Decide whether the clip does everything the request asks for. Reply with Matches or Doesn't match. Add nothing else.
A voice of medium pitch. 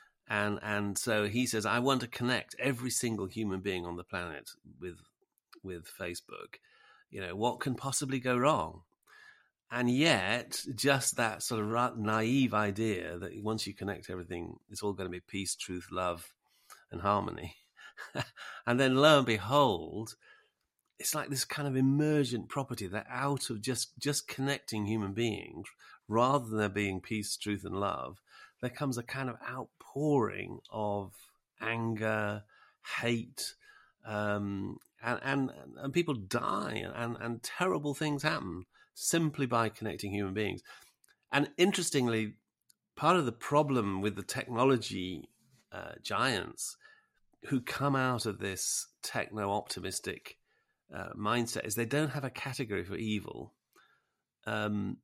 Doesn't match